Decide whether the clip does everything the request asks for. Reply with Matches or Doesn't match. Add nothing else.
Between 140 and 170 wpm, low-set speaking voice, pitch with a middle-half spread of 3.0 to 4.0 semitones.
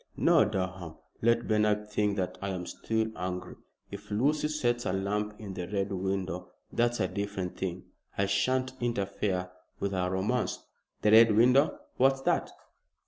Matches